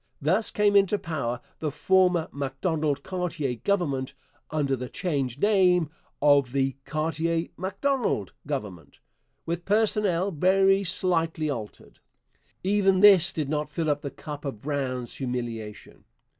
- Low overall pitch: No, medium, 155 Hz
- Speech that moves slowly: Yes, slow, 125 wpm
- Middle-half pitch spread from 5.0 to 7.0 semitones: Yes, wide, 5.4 semitones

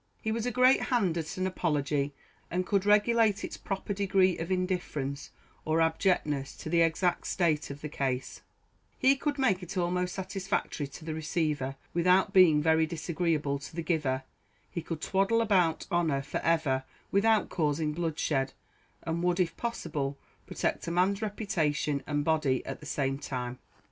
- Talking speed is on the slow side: No, average, 165 wpm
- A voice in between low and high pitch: Yes, medium, 165 Hz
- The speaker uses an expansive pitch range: No, average, 4.2 semitones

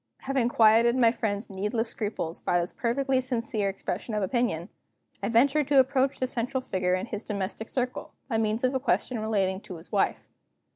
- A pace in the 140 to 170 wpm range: No, average, 185 wpm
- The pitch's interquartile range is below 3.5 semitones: No, average, 4.1 semitones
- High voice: Yes, high, 225 Hz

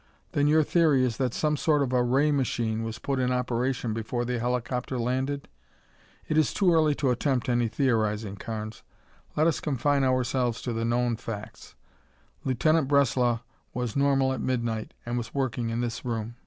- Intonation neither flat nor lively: Yes, average, 3.1 semitones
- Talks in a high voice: No, low, 125 Hz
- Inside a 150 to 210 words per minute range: Yes, average, 175 wpm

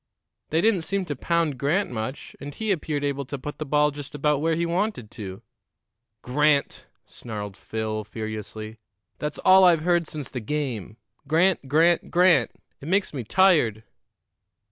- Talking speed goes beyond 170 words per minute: No, average, 160 wpm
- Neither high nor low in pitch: Yes, medium, 150 Hz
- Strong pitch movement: Yes, wide, 6.1 semitones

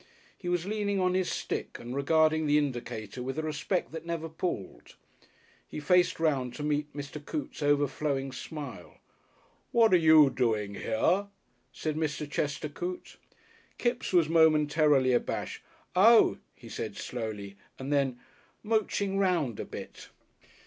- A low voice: No, medium, 150 Hz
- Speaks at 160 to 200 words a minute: No, average, 140 wpm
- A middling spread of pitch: Yes, average, 4.7 semitones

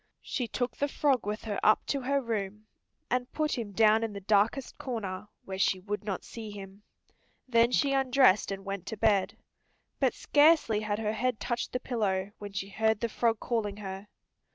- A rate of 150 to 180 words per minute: No, average, 190 wpm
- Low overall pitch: No, high, 215 Hz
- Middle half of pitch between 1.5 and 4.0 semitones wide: Yes, average, 3.5 semitones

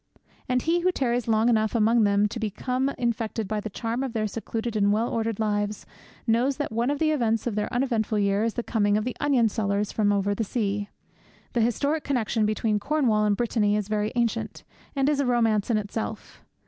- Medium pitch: No, high, 225 Hz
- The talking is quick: Yes, fast, 210 wpm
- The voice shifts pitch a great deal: No, narrow, 2.5 semitones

